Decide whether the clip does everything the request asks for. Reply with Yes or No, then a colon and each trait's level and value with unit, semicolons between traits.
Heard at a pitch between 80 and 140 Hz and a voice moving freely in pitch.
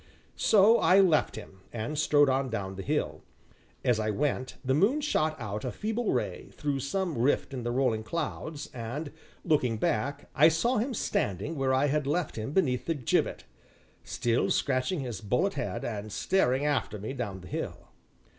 Yes: low, 135 Hz; wide, 5.7 semitones